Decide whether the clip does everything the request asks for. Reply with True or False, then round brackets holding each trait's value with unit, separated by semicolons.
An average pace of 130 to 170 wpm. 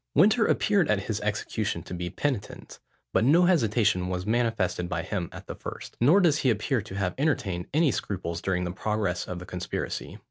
False (190 wpm)